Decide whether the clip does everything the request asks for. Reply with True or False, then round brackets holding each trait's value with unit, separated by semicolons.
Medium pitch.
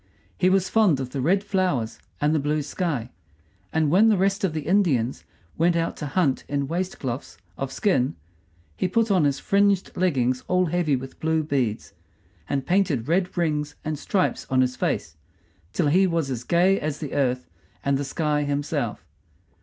True (155 Hz)